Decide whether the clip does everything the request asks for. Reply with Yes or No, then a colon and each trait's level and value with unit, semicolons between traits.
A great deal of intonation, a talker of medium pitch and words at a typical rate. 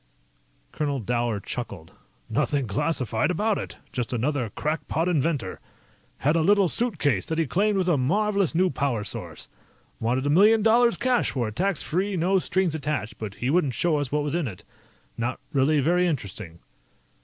Yes: wide, 6.7 semitones; medium, 150 Hz; average, 170 wpm